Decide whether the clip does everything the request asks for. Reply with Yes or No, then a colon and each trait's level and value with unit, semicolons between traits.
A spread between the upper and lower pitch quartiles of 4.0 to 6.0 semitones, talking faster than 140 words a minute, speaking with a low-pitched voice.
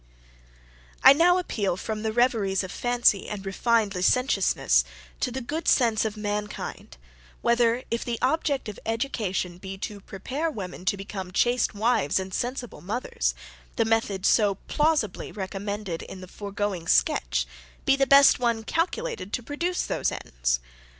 No: average, 4.4 semitones; average, 150 wpm; high, 215 Hz